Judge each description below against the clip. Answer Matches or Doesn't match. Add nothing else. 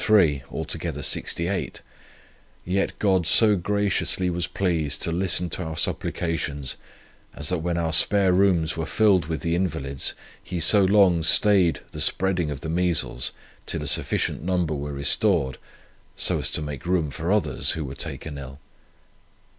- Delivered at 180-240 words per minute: Doesn't match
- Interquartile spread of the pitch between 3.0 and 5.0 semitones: Matches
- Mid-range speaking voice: Doesn't match